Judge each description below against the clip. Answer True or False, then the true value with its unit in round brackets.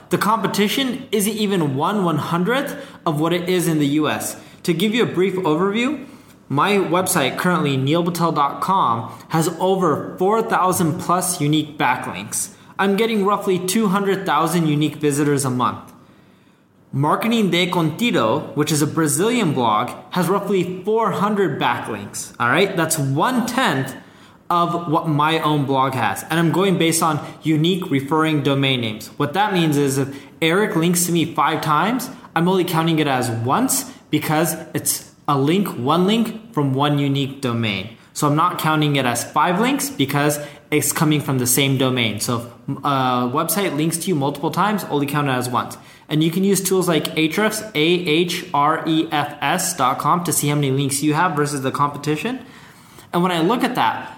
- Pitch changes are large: False (4.4 semitones)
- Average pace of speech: True (165 wpm)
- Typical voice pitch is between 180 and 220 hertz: False (160 Hz)